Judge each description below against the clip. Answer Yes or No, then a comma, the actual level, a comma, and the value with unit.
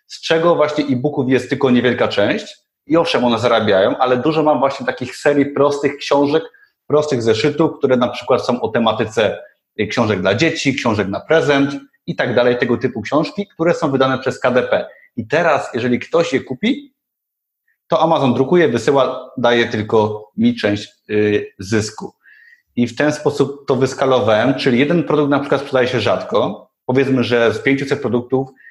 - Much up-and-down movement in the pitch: No, average, 4.1 semitones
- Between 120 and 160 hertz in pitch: Yes, low, 135 Hz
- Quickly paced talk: Yes, fast, 165 wpm